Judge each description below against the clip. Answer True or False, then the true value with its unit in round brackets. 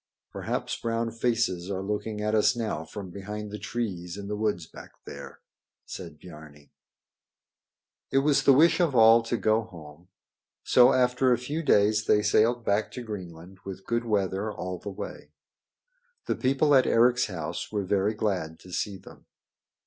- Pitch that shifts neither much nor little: True (4.1 semitones)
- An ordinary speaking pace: True (165 wpm)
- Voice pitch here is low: True (105 Hz)